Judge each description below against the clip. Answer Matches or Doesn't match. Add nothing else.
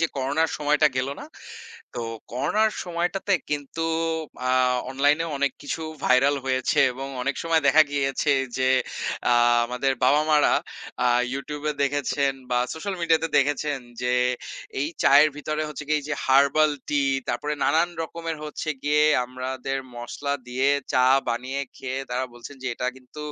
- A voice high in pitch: Doesn't match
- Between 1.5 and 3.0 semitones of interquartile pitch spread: Matches